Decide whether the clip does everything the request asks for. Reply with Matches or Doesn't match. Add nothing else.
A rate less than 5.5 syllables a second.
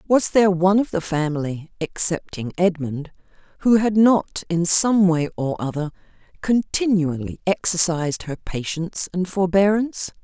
Matches